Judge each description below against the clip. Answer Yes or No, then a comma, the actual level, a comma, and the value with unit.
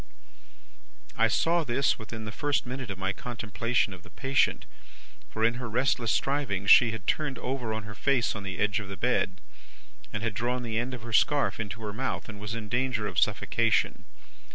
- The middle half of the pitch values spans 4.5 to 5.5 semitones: No, average, 3.2 semitones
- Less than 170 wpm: No, average, 195 wpm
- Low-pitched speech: Yes, low, 115 Hz